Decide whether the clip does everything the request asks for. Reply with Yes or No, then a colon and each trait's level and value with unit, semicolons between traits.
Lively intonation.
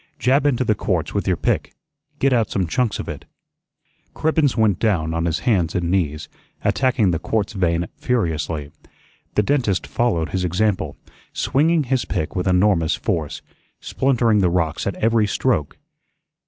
Yes: wide, 6.3 semitones